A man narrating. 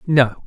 Yes: male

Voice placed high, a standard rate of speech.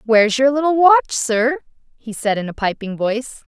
Yes: high, 240 Hz; average, 185 wpm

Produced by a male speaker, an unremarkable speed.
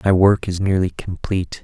Yes: male; average, 185 wpm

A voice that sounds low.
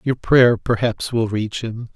Yes: low, 115 Hz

